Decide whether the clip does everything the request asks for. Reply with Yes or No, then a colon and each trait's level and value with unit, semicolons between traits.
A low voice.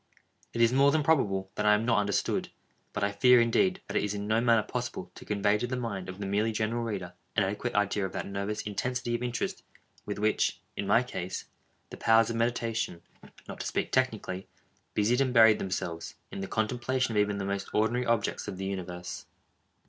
Yes: low, 105 Hz